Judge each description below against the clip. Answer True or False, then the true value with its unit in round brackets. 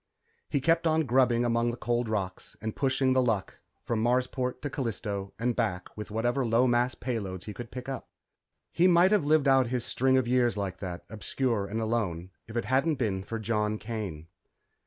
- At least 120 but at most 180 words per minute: False (195 wpm)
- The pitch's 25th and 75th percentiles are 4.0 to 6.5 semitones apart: False (3.5 semitones)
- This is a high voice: False (120 Hz)